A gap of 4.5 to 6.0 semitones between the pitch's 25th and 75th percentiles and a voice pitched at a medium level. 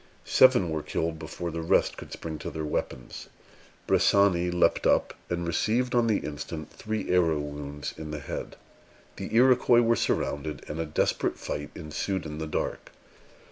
No: average, 4.8 semitones; very low, 80 Hz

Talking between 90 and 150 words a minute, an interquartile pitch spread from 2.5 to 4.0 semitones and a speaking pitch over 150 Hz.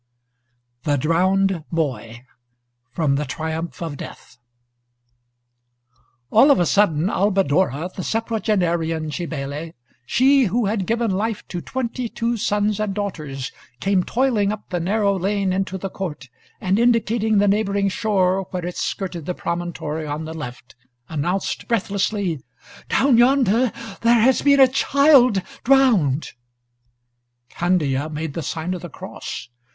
No: slow, 135 wpm; average, 5.3 semitones; high, 190 Hz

